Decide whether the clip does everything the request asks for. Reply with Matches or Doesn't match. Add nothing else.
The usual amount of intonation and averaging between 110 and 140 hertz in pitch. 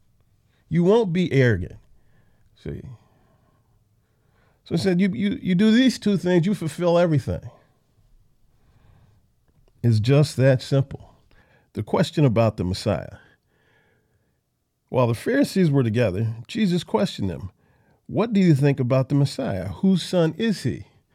Doesn't match